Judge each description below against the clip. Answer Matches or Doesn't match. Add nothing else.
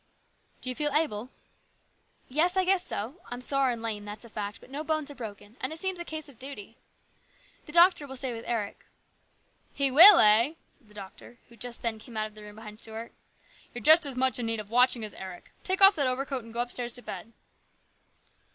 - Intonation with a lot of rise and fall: Doesn't match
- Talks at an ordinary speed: Doesn't match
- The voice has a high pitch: Matches